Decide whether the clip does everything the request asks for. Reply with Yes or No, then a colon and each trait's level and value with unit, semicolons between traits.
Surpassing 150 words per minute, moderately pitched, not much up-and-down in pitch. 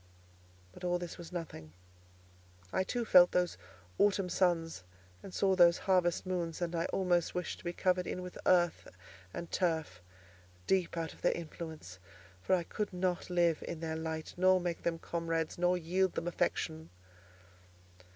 Yes: average, 160 wpm; medium, 175 Hz; narrow, 1.7 semitones